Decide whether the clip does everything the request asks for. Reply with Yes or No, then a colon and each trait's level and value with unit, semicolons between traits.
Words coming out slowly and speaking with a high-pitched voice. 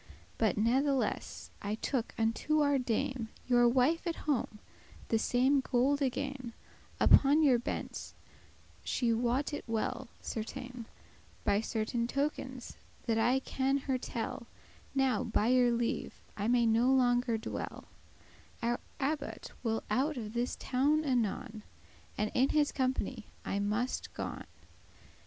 Yes: slow, 130 wpm; high, 245 Hz